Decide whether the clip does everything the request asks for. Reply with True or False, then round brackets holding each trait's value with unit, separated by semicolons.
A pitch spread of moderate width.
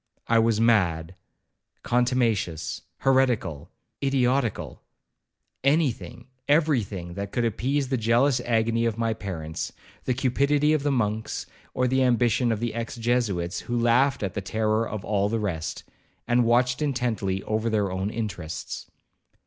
True (3.8 semitones)